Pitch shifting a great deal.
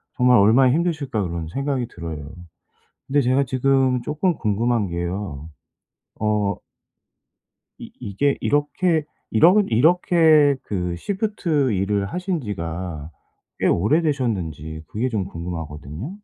Yes: wide, 8.5 semitones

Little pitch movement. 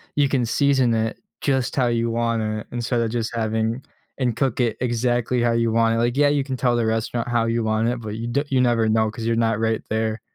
Yes: narrow, 1.5 semitones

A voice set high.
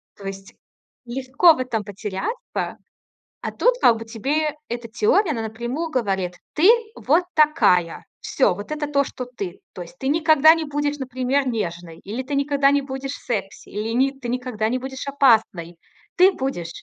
Yes: very high, 255 Hz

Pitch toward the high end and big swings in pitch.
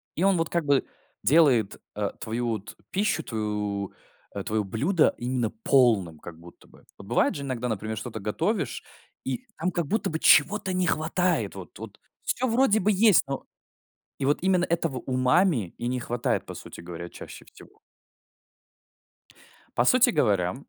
No: low, 130 Hz; wide, 8.5 semitones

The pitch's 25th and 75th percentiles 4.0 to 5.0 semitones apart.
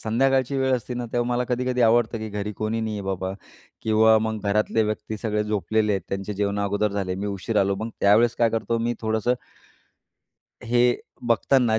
No: narrow, 2.5 semitones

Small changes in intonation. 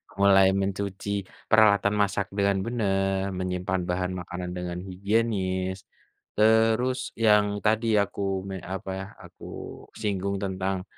Yes: narrow, 1.8 semitones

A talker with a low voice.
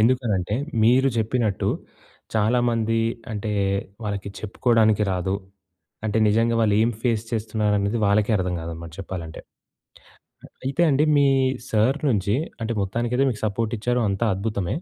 Yes: low, 110 Hz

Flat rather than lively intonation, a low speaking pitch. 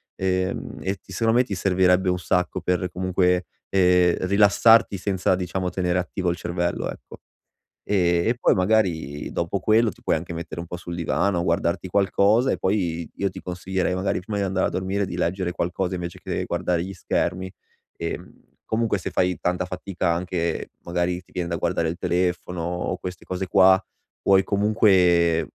Yes: narrow, 1.7 semitones; very low, 90 Hz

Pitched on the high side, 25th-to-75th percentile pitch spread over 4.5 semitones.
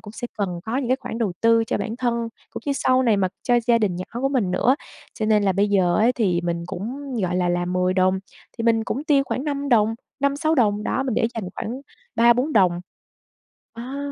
Yes: high, 225 Hz; average, 5.1 semitones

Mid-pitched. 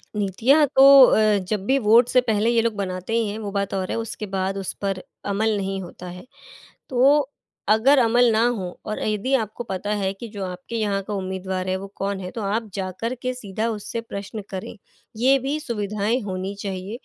No: high, 210 Hz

